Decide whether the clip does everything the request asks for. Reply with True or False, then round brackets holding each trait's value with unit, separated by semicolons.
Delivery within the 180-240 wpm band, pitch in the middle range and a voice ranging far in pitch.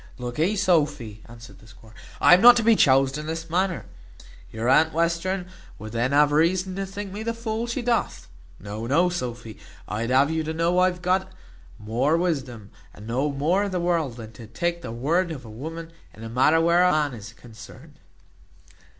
True (200 wpm; 155 Hz; 7.1 semitones)